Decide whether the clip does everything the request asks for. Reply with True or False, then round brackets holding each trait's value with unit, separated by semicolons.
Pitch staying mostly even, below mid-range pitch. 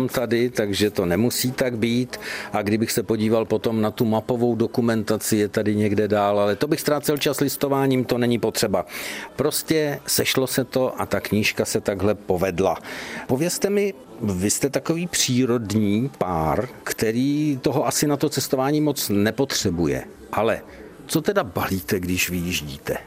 False (4.7 semitones; 120 Hz)